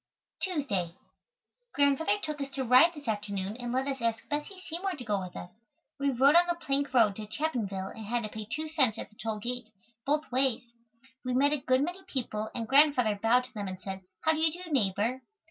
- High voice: Yes, very high, 255 Hz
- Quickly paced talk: Yes, fast, 215 wpm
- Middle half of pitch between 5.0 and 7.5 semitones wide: Yes, average, 5.3 semitones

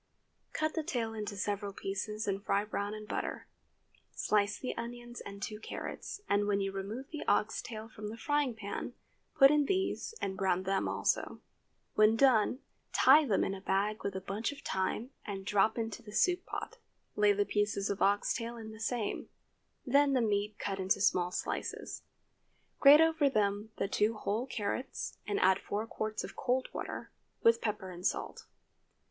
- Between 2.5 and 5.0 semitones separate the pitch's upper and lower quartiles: Yes, average, 3.1 semitones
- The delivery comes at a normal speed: Yes, average, 180 wpm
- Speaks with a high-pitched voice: Yes, high, 215 Hz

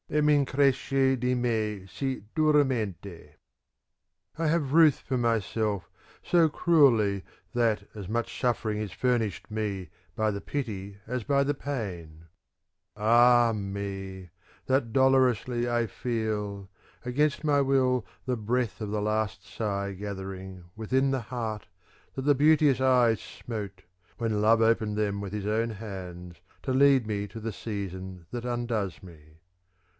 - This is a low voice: Yes, low, 110 Hz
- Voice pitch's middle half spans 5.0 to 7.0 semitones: No, average, 4.4 semitones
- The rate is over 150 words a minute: No, average, 145 wpm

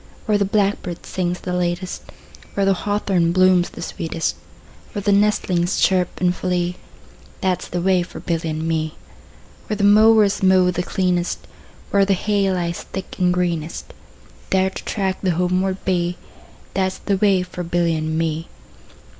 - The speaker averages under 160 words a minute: No, average, 170 wpm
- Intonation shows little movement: Yes, narrow, 1.9 semitones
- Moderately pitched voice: Yes, medium, 180 Hz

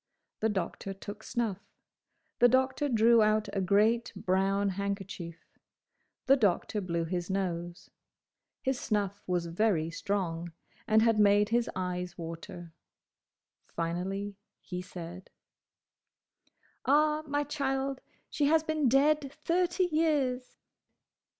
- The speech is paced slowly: Yes, slow, 110 wpm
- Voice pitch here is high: Yes, high, 205 Hz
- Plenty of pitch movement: Yes, wide, 6.4 semitones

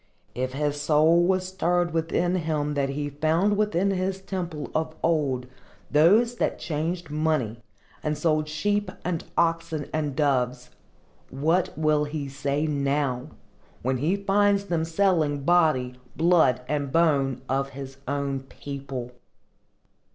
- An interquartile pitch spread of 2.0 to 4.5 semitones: Yes, average, 3.7 semitones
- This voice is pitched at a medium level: Yes, medium, 155 Hz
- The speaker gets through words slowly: Yes, slow, 130 wpm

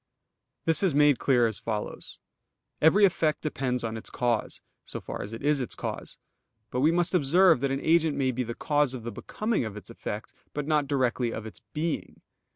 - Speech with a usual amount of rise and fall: Yes, average, 4.9 semitones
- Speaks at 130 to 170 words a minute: No, average, 200 wpm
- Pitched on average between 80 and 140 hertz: Yes, low, 135 Hz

